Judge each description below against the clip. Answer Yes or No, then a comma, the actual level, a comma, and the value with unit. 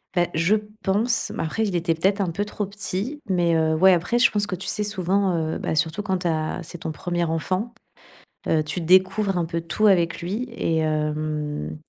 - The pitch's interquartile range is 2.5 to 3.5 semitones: No, average, 3.9 semitones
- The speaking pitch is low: No, medium, 175 Hz